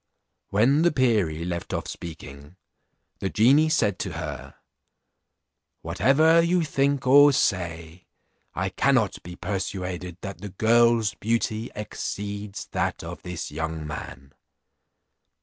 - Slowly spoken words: Yes, slow, 115 wpm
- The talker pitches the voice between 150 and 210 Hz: No, low, 100 Hz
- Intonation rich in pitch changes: Yes, wide, 6.5 semitones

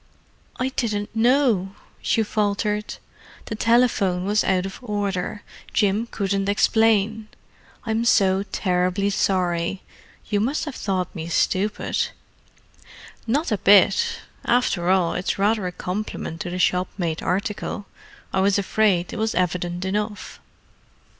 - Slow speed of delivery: Yes, slow, 120 wpm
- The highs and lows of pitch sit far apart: No, average, 3.0 semitones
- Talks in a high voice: Yes, high, 200 Hz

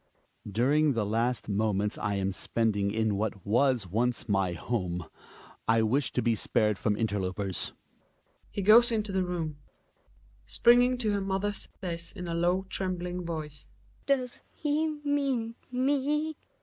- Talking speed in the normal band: Yes, average, 145 wpm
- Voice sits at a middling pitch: Yes, medium, 150 Hz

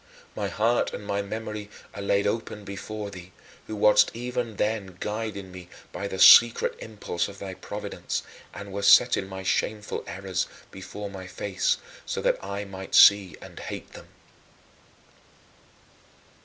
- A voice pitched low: Yes, low, 100 Hz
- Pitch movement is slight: Yes, narrow, 1.8 semitones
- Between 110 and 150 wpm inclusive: Yes, average, 145 wpm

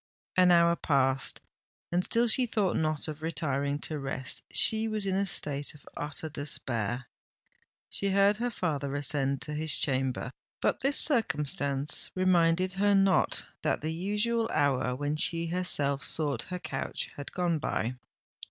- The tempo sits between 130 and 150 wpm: Yes, average, 145 wpm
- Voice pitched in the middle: Yes, medium, 160 Hz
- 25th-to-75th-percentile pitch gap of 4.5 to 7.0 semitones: Yes, average, 5.1 semitones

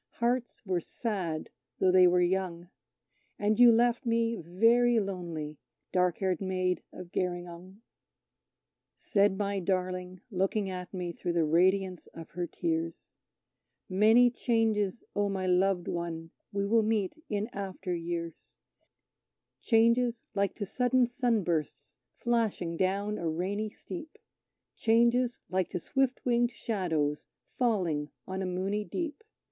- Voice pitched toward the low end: No, high, 190 Hz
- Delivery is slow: Yes, slow, 130 wpm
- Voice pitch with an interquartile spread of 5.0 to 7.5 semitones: No, average, 4.3 semitones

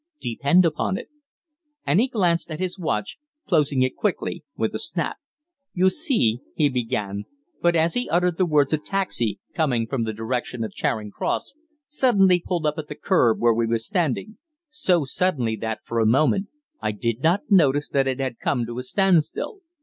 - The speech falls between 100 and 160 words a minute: No, average, 190 wpm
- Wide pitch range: Yes, wide, 7.5 semitones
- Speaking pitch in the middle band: Yes, medium, 150 Hz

